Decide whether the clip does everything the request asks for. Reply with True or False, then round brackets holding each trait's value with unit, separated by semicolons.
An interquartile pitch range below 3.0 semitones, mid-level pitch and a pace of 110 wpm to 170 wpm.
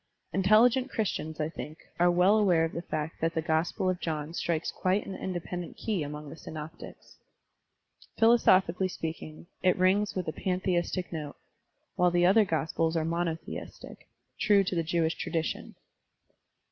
True (2.6 semitones; 175 Hz; 150 wpm)